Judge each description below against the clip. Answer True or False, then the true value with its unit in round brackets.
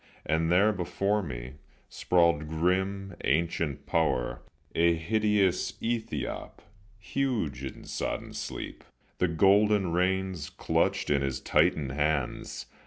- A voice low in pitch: True (85 Hz)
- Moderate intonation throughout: True (4.9 semitones)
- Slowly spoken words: True (105 wpm)